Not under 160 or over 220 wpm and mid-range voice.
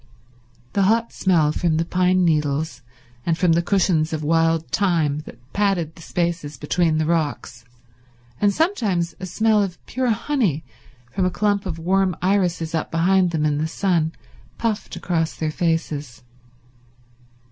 No: average, 150 wpm; medium, 170 Hz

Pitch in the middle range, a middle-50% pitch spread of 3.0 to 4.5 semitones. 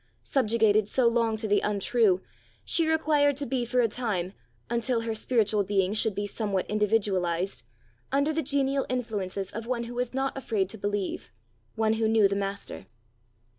No: high, 220 Hz; average, 3.7 semitones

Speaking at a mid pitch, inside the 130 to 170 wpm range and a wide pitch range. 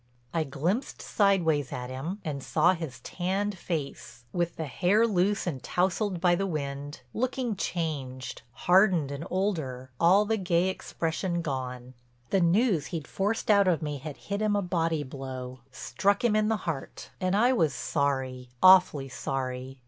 Yes: medium, 170 Hz; average, 160 wpm; wide, 5.9 semitones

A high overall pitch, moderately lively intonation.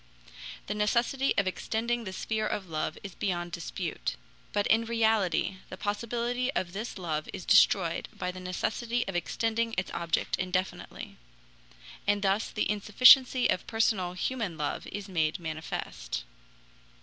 Yes: high, 200 Hz; average, 4.2 semitones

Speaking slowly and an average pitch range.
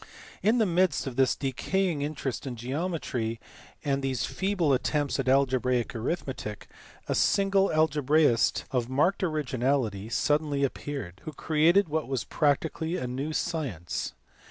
Yes: slow, 130 wpm; average, 3.9 semitones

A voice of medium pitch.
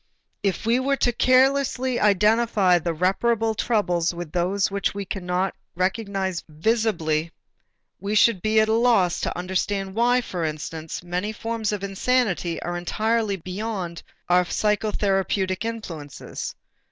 No: high, 200 Hz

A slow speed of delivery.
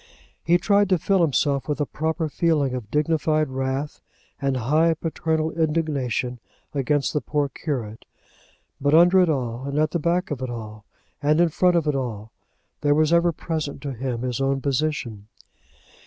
No: average, 170 wpm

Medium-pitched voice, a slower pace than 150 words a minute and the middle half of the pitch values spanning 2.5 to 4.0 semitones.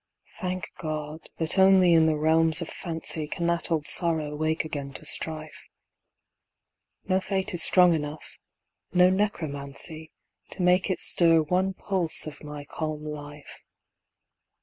Yes: medium, 160 Hz; average, 140 wpm; average, 2.9 semitones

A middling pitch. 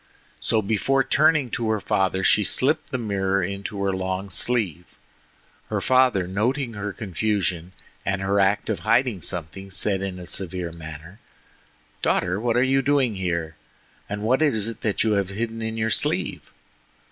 No: low, 100 Hz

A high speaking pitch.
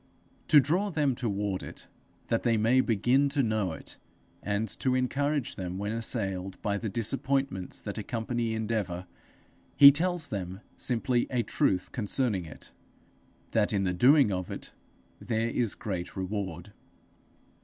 No: low, 110 Hz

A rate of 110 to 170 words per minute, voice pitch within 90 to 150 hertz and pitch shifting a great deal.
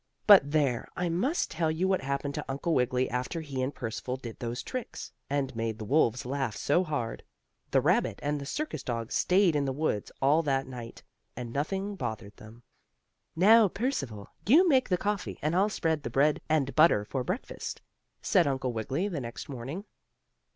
No: average, 185 wpm; medium, 140 Hz; wide, 6.0 semitones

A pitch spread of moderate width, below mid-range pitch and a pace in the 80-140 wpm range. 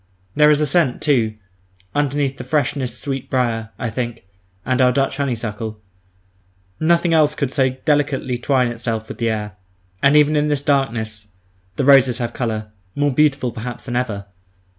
No: average, 3.7 semitones; low, 130 Hz; average, 160 wpm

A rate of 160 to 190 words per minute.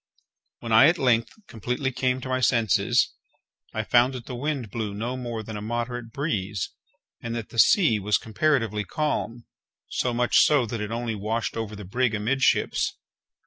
Yes: average, 175 wpm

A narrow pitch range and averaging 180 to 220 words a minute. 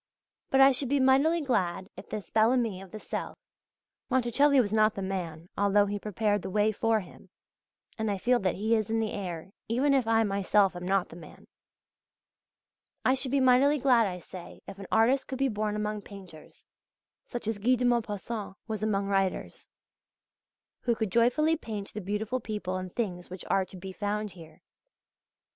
No: average, 3.8 semitones; average, 190 wpm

